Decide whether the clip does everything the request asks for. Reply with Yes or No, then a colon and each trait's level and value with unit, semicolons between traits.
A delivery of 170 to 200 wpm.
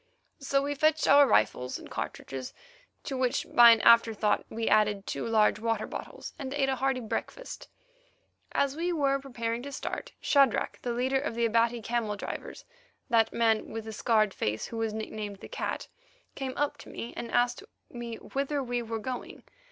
Yes: average, 180 wpm